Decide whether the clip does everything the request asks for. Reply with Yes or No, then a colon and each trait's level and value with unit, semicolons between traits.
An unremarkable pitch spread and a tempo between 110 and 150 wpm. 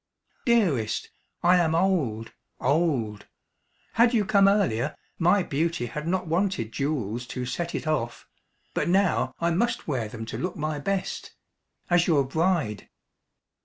No: wide, 6.8 semitones; average, 140 wpm